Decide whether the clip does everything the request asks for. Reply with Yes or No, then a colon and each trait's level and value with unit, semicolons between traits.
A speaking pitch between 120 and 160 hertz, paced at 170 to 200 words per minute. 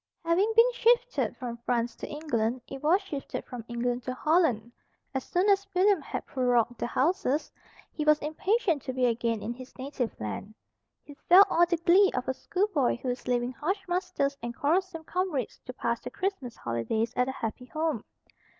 No: very high, 275 Hz; average, 185 wpm